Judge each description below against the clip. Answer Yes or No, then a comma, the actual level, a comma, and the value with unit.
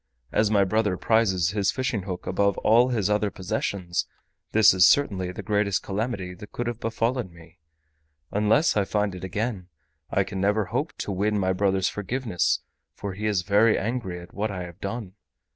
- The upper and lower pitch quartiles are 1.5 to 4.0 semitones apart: Yes, average, 2.7 semitones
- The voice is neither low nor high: No, low, 100 Hz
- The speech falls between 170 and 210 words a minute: Yes, average, 175 wpm